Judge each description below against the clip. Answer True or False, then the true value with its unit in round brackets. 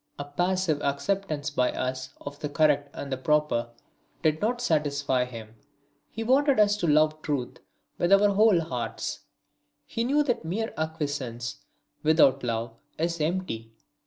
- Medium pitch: True (155 Hz)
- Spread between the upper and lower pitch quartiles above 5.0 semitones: True (5.4 semitones)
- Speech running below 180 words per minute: True (145 wpm)